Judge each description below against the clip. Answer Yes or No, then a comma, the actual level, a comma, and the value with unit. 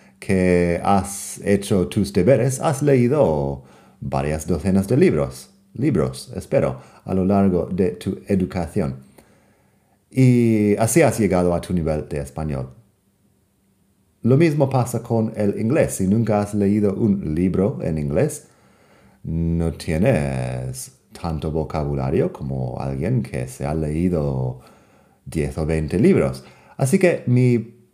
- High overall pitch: No, very low, 90 Hz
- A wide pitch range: Yes, wide, 6.1 semitones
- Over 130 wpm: No, slow, 125 wpm